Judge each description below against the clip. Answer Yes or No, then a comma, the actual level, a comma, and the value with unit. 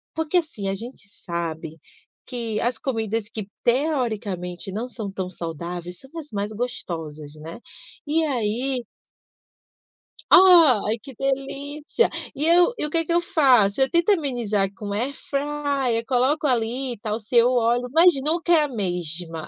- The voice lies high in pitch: Yes, high, 240 Hz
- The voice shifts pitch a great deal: Yes, wide, 6.1 semitones